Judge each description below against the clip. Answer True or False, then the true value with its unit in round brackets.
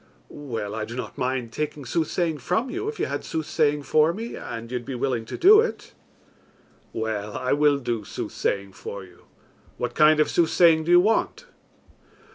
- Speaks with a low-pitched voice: False (145 Hz)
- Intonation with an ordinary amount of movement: False (6.1 semitones)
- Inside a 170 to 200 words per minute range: True (180 wpm)